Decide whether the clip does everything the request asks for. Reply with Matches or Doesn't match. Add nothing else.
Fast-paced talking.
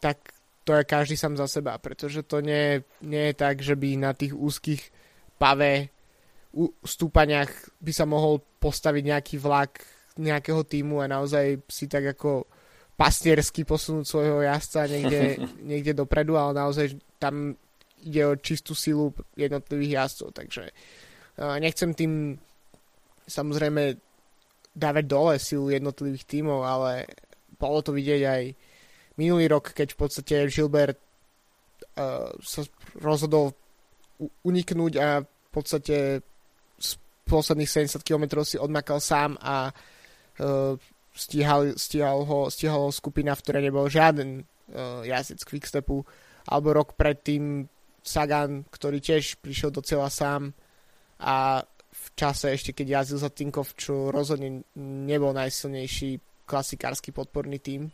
Doesn't match